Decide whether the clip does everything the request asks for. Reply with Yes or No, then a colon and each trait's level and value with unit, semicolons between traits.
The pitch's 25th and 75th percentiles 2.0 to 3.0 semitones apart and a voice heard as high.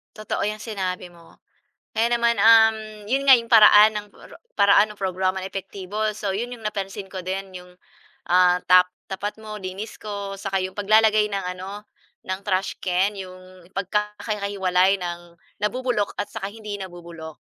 Yes: narrow, 2.4 semitones; high, 200 Hz